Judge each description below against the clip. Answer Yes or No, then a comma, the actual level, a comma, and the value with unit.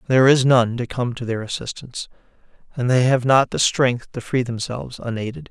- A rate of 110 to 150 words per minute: No, average, 195 wpm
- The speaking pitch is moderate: No, low, 125 Hz